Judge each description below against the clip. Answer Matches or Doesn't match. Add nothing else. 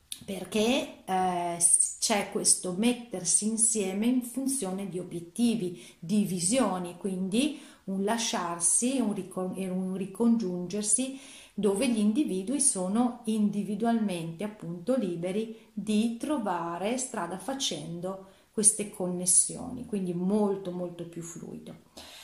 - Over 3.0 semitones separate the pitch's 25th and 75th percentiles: Matches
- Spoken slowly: Matches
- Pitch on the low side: Doesn't match